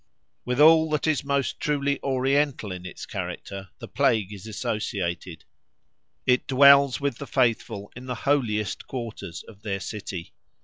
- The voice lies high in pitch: No, low, 125 Hz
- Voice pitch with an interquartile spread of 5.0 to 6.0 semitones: Yes, wide, 5.5 semitones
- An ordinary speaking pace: Yes, average, 145 wpm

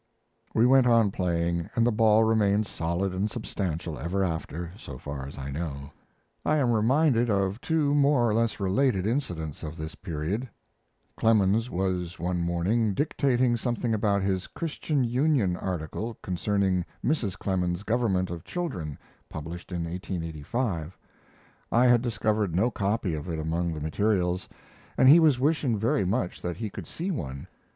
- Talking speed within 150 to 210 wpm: Yes, average, 155 wpm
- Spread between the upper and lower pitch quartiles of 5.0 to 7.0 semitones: Yes, wide, 5.5 semitones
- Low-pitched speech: Yes, low, 100 Hz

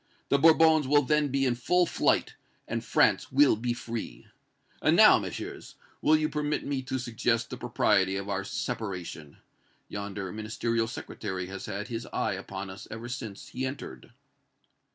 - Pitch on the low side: Yes, low, 115 Hz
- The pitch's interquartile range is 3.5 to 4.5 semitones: No, wide, 5.5 semitones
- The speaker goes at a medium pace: Yes, average, 160 wpm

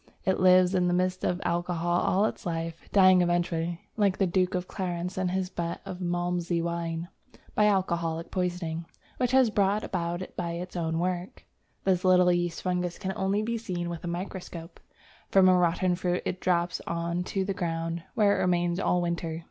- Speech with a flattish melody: Yes, narrow, 1.5 semitones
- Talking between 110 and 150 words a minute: No, average, 190 wpm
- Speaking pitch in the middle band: Yes, medium, 180 Hz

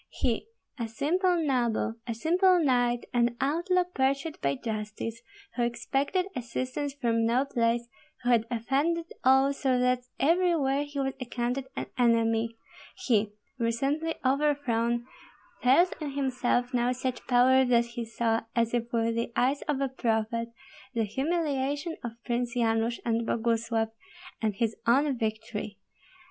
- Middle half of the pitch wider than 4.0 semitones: No, average, 3.3 semitones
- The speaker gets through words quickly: No, average, 140 wpm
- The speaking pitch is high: Yes, high, 245 Hz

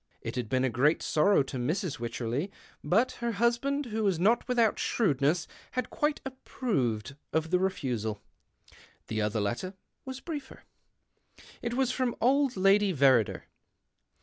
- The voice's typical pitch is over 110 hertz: Yes, medium, 185 Hz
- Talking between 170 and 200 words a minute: No, average, 145 wpm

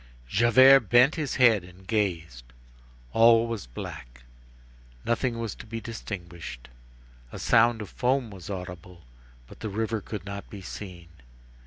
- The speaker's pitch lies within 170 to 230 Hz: No, low, 105 Hz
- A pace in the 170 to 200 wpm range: No, average, 140 wpm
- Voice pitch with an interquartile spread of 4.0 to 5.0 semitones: Yes, average, 4.5 semitones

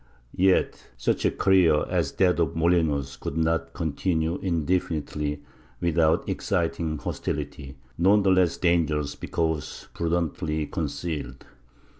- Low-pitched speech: Yes, very low, 80 Hz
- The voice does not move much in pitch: Yes, narrow, 2.3 semitones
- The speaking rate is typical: No, slow, 110 wpm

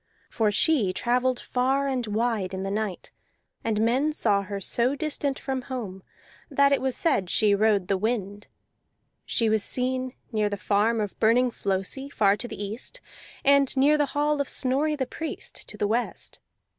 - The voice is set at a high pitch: Yes, high, 235 Hz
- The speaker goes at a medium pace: Yes, average, 175 wpm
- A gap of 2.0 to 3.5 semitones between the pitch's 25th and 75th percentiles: No, average, 4.6 semitones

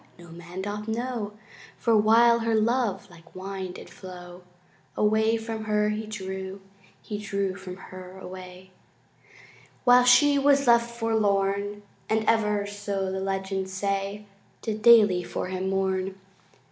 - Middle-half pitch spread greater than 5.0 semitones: No, average, 2.7 semitones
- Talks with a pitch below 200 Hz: No, high, 205 Hz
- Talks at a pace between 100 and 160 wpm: Yes, slow, 135 wpm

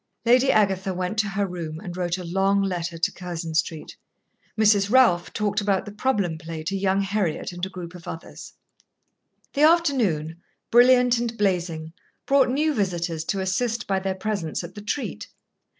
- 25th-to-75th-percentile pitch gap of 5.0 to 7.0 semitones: No, average, 3.8 semitones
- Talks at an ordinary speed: Yes, average, 170 wpm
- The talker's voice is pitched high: Yes, high, 195 Hz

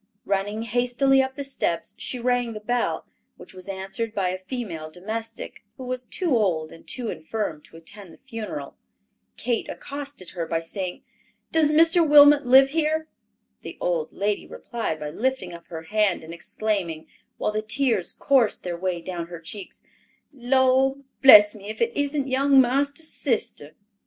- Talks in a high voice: Yes, high, 225 Hz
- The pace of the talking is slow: No, average, 165 wpm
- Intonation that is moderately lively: No, wide, 6.6 semitones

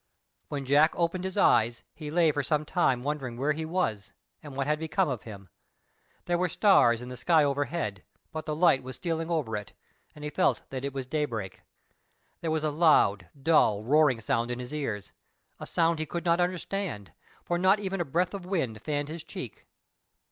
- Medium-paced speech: Yes, average, 195 wpm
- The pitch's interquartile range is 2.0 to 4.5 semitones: No, average, 5.0 semitones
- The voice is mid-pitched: Yes, medium, 150 Hz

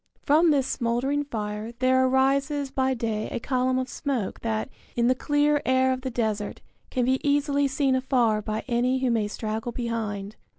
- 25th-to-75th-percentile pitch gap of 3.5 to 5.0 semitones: No, average, 3.1 semitones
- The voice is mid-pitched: No, very high, 255 Hz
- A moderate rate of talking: Yes, average, 175 wpm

